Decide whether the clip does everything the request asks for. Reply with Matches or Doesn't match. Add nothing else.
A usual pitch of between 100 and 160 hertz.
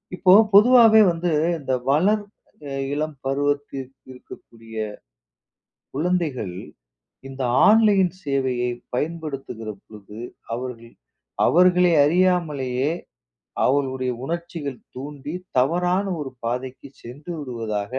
Matches